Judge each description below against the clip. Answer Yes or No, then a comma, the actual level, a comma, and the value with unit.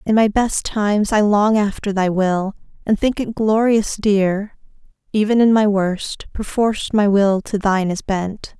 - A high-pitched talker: Yes, high, 205 Hz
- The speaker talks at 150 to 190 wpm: Yes, average, 175 wpm